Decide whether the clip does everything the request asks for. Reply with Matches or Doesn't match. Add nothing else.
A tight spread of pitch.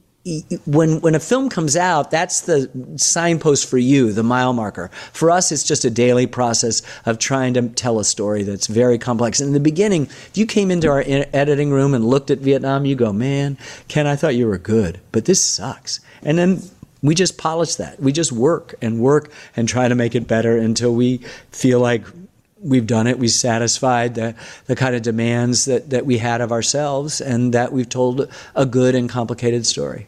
Doesn't match